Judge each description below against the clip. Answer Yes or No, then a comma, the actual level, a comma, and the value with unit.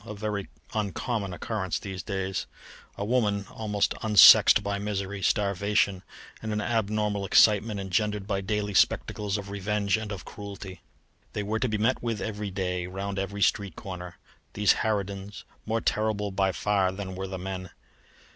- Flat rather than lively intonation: Yes, narrow, 1.5 semitones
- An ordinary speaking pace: Yes, average, 155 wpm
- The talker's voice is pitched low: Yes, low, 100 Hz